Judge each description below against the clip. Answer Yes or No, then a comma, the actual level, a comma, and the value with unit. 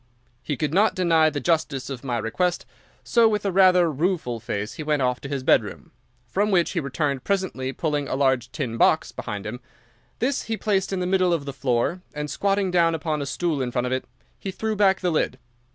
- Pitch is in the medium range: Yes, medium, 155 Hz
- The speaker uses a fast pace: Yes, fast, 215 wpm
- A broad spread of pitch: Yes, wide, 5.9 semitones